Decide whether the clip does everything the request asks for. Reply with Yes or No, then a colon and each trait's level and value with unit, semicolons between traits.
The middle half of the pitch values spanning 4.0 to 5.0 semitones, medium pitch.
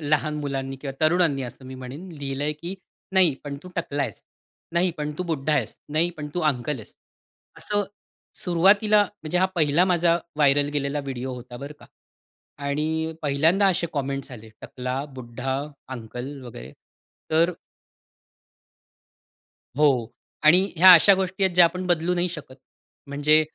Yes: average, 4.3 semitones; medium, 150 Hz